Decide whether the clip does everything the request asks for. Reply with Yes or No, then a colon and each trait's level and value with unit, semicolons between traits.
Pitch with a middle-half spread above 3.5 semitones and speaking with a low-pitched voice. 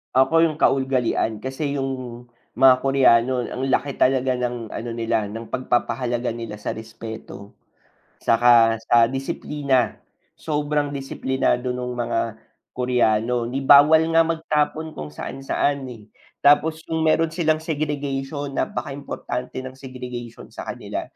No: average, 3.2 semitones; low, 130 Hz